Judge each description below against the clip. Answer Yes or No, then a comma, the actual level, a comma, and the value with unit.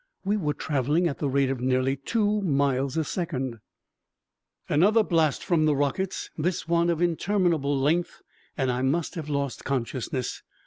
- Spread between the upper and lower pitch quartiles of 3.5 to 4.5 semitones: Yes, average, 4.2 semitones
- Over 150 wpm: Yes, average, 160 wpm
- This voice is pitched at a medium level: Yes, medium, 150 Hz